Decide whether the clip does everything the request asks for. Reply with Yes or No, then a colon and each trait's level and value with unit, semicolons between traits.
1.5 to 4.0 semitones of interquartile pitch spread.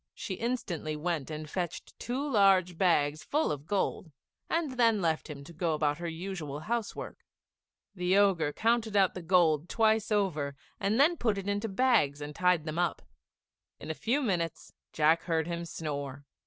No: average, 5.3 semitones